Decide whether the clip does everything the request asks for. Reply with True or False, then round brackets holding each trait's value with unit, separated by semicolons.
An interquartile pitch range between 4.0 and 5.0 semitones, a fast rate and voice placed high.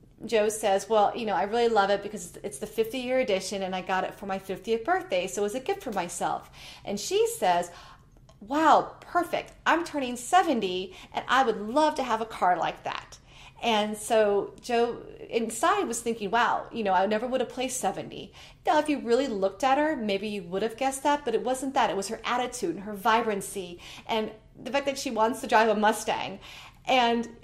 True (4.5 semitones; 215 wpm; 225 Hz)